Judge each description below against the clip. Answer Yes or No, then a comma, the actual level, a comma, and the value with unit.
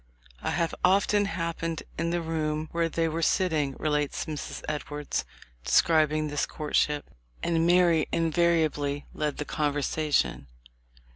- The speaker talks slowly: Yes, slow, 125 wpm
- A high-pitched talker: No, medium, 155 Hz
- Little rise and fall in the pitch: Yes, narrow, 2.1 semitones